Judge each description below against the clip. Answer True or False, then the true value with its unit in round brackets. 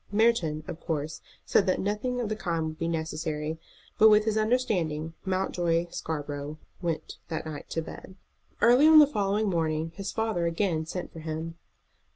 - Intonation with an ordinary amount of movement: True (5.0 semitones)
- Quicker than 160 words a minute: True (170 wpm)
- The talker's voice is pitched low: False (170 Hz)